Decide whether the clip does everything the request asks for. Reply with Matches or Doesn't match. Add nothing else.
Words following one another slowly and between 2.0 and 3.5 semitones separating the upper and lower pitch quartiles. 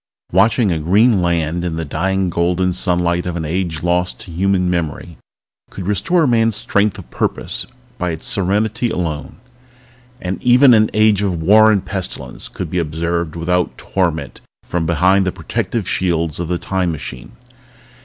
Doesn't match